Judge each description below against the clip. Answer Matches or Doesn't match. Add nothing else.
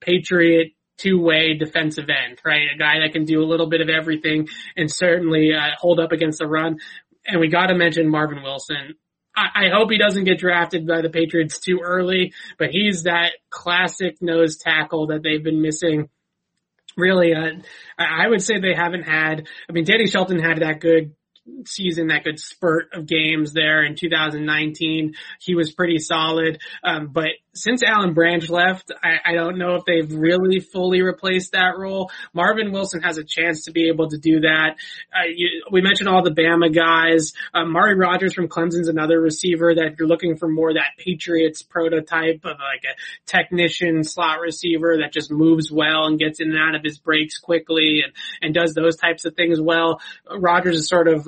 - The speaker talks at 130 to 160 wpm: Doesn't match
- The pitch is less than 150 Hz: Doesn't match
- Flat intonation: Matches